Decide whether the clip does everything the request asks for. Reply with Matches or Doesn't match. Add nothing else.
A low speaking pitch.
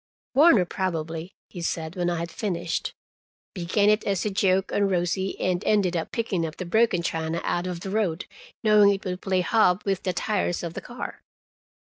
Doesn't match